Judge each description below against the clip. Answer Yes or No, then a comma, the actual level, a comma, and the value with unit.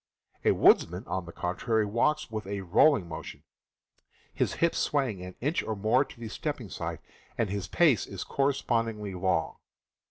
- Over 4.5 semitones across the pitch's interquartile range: Yes, wide, 5.5 semitones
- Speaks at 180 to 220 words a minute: No, average, 160 wpm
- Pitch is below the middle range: Yes, low, 110 Hz